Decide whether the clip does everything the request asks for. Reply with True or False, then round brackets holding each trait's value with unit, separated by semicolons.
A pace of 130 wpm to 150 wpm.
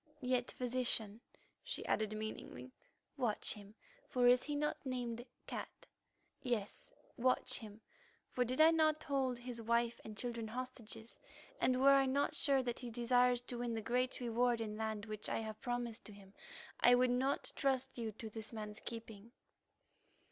False (165 wpm)